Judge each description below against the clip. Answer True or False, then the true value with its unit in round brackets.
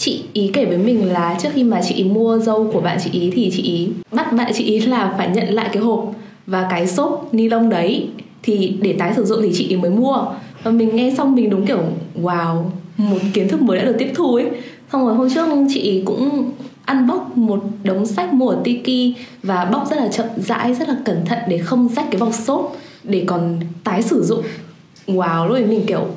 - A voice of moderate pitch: False (220 Hz)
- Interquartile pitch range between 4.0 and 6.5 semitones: True (4.5 semitones)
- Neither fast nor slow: True (235 wpm)